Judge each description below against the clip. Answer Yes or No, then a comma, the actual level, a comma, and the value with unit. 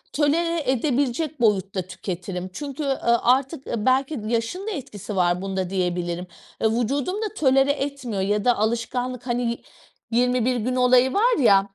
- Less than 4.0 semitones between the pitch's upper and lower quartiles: No, average, 5.2 semitones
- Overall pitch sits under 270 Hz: Yes, high, 245 Hz